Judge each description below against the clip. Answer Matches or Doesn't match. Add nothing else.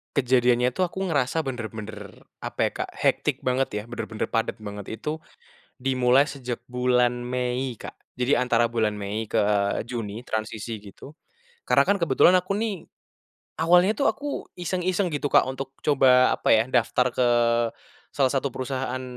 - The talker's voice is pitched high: Doesn't match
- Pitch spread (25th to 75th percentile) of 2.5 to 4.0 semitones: Matches